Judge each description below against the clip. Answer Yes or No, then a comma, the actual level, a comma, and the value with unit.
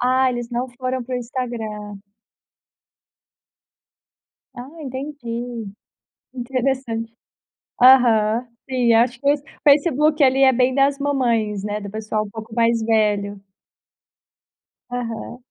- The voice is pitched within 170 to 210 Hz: No, high, 245 Hz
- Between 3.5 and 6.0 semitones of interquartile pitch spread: No, average, 2.7 semitones